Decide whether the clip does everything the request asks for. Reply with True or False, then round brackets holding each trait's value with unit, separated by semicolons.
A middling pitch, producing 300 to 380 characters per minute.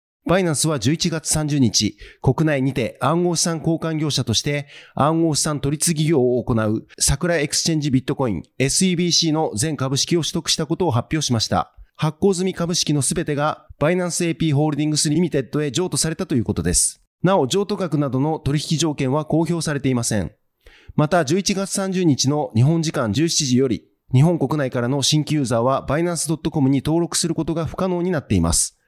False (155 Hz; 395 characters per minute)